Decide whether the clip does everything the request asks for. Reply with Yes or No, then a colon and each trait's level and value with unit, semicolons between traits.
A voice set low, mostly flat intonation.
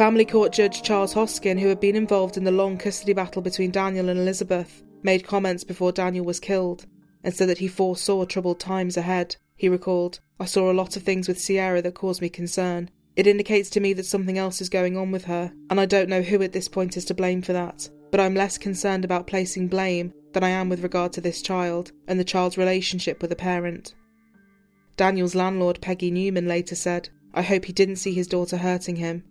No: medium, 185 Hz; narrow, 1.4 semitones